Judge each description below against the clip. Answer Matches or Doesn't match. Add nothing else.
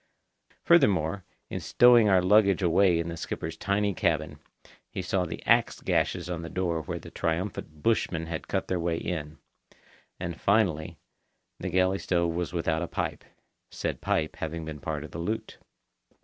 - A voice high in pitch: Doesn't match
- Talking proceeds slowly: Doesn't match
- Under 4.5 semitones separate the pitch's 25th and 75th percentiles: Matches